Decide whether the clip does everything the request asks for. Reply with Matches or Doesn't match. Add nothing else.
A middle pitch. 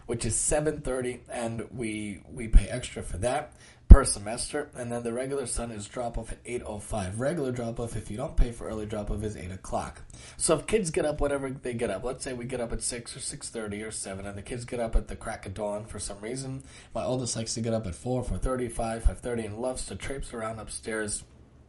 Doesn't match